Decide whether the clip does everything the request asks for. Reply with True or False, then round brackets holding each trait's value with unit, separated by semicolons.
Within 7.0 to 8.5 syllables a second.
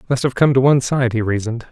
True (7.3 syllables/s)